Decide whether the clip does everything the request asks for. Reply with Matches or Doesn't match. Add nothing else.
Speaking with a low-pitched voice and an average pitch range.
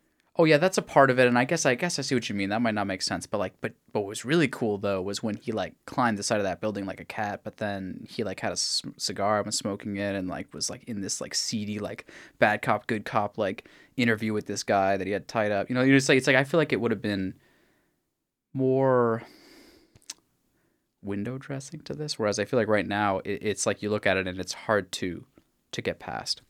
Matches